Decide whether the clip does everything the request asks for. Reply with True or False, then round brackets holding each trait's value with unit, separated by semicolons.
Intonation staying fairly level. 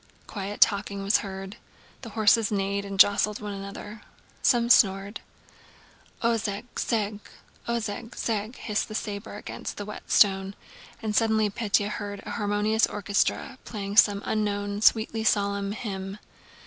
True (1.5 semitones)